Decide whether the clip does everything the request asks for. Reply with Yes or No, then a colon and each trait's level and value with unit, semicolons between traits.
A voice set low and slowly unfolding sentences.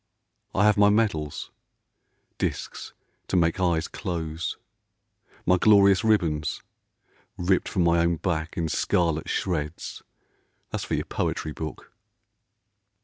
Yes: very low, 85 Hz; slow, 125 wpm